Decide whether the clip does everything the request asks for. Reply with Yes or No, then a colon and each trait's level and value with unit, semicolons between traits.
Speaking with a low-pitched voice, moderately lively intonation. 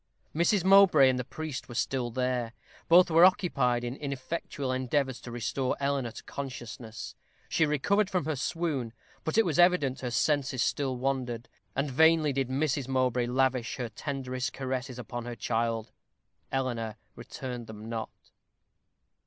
Yes: low, 130 Hz; average, 3.5 semitones